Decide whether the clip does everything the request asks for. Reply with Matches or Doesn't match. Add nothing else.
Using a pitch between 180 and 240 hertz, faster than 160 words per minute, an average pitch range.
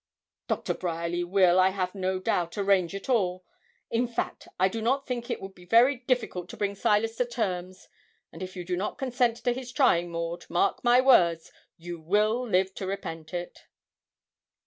Matches